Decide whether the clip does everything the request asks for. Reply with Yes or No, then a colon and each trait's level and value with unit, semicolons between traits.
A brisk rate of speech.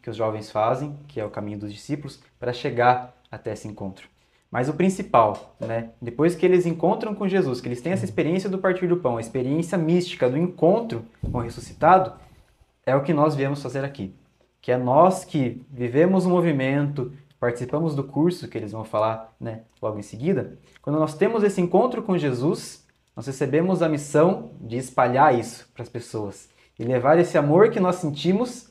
Yes: fast, 190 wpm